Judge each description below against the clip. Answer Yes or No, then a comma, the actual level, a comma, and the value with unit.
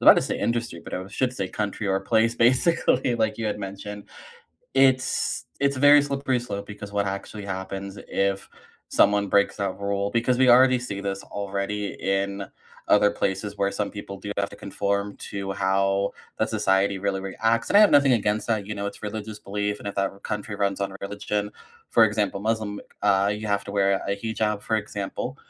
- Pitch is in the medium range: No, low, 100 Hz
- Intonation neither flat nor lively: No, narrow, 2.1 semitones